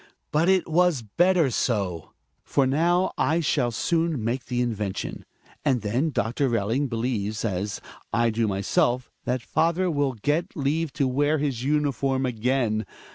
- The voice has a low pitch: Yes, low, 130 Hz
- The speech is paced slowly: No, average, 145 wpm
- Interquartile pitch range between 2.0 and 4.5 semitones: No, average, 5.0 semitones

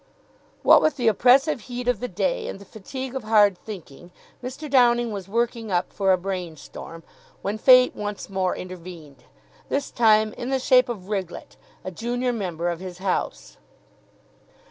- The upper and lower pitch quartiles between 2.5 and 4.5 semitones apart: No, average, 5.1 semitones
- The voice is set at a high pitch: Yes, high, 215 Hz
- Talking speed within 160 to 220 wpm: Yes, average, 165 wpm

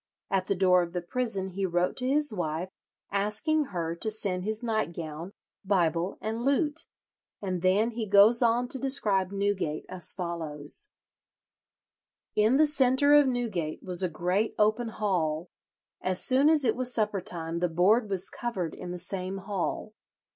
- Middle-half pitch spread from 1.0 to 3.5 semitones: No, average, 4.9 semitones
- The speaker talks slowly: No, average, 160 wpm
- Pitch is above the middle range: Yes, high, 195 Hz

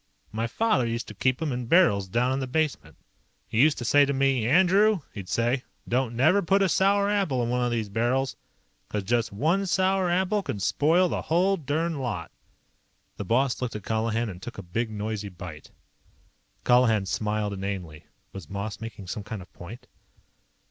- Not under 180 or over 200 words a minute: Yes, average, 185 wpm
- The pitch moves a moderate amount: No, wide, 7.1 semitones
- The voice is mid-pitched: No, low, 120 Hz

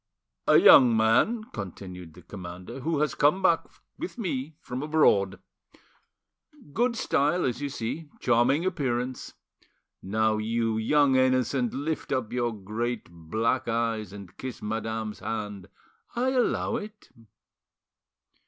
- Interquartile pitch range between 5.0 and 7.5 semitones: Yes, average, 5.3 semitones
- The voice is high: No, low, 120 Hz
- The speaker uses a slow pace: Yes, slow, 125 wpm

